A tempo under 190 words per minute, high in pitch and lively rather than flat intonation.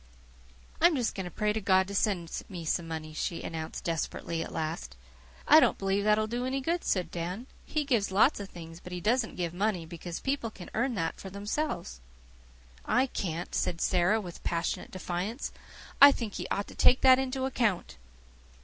No: average, 195 wpm; high, 195 Hz; wide, 5.7 semitones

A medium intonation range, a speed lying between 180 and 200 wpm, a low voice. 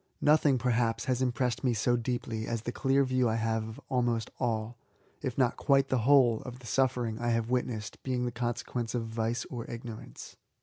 No: narrow, 2.0 semitones; average, 190 wpm; low, 120 Hz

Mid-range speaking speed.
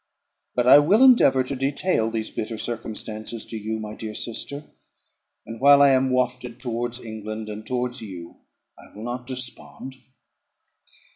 Yes: average, 150 wpm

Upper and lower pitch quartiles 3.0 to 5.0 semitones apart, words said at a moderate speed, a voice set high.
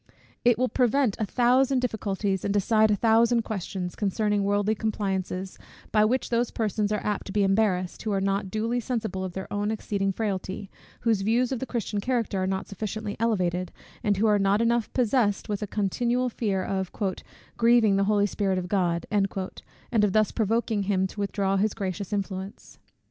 No: narrow, 2.6 semitones; average, 180 wpm; high, 205 Hz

